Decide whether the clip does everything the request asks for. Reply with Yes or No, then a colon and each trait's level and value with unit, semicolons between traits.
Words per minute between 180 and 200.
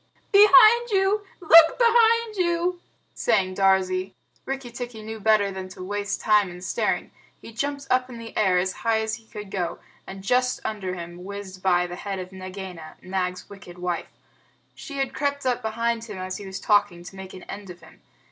Yes: average, 190 wpm